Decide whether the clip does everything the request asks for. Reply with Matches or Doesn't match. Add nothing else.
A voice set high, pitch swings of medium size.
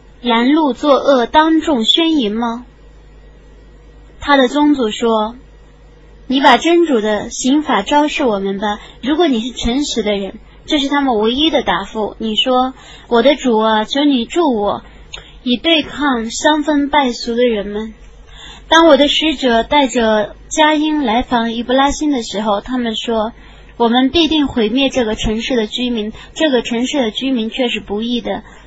Matches